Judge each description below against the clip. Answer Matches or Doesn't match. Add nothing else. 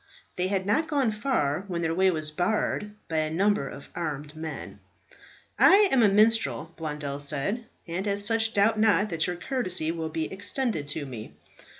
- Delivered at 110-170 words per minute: Doesn't match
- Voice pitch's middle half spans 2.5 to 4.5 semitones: Doesn't match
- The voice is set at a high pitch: Doesn't match